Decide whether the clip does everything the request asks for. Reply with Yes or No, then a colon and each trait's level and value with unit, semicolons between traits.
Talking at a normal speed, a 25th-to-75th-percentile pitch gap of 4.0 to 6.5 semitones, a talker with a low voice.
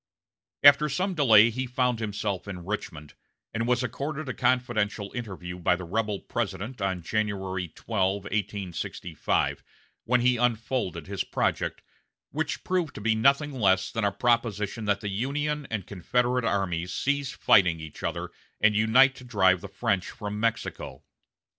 Yes: average, 150 wpm; average, 4.4 semitones; low, 110 Hz